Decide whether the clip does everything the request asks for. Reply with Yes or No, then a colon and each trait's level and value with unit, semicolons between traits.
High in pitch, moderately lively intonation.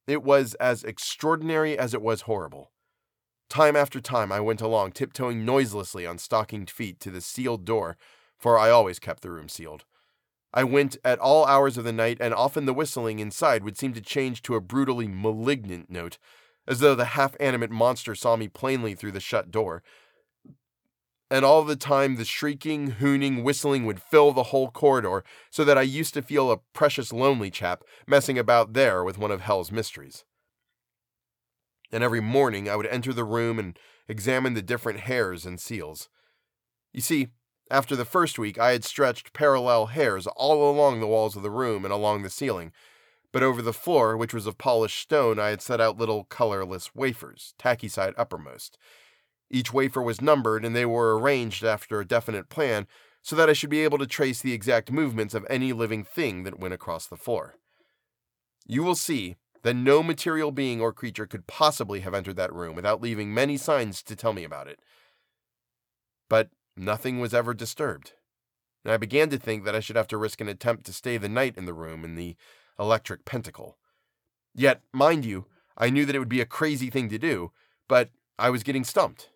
No: low, 120 Hz; average, 4.2 semitones